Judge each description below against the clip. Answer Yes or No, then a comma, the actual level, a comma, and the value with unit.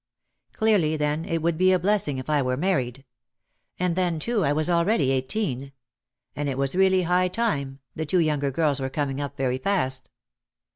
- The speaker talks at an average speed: Yes, average, 185 wpm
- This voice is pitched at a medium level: Yes, medium, 155 Hz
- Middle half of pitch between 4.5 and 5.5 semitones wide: Yes, average, 5.0 semitones